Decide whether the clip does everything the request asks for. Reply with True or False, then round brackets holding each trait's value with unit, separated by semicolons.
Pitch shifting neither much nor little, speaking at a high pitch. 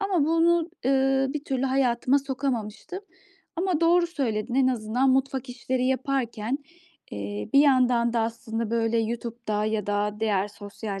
True (3.6 semitones; 250 Hz)